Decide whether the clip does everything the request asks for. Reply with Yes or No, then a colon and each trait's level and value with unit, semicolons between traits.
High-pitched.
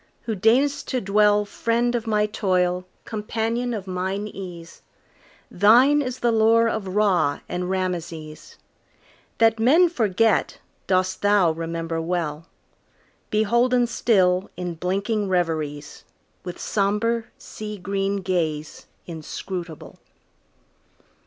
Yes: high, 200 Hz